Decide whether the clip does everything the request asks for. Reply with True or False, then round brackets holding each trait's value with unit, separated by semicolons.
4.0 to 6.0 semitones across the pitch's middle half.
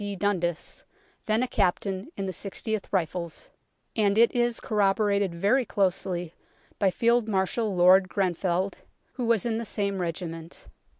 False (3.2 semitones)